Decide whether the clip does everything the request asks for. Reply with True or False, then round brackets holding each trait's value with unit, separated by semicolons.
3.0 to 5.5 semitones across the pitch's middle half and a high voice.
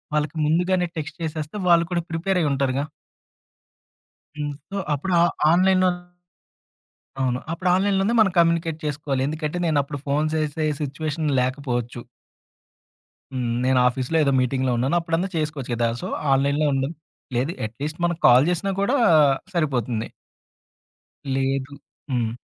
False (4.2 semitones; 150 Hz)